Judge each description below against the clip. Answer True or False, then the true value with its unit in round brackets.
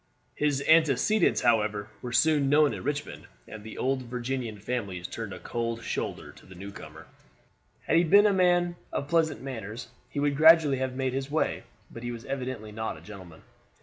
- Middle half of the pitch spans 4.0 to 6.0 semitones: True (5.0 semitones)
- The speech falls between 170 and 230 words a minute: True (180 wpm)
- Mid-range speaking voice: False (130 Hz)